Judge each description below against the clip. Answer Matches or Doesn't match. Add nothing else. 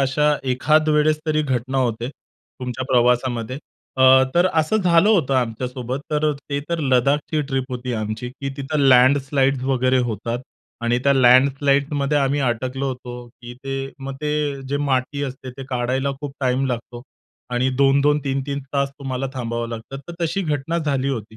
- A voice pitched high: Doesn't match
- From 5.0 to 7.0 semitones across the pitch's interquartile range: Doesn't match